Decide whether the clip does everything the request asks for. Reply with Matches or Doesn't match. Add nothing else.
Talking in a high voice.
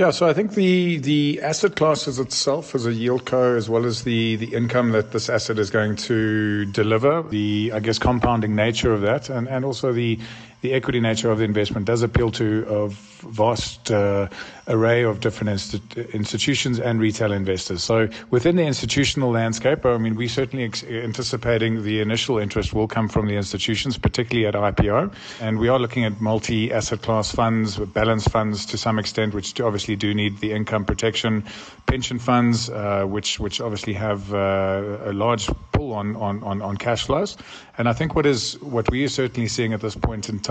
Doesn't match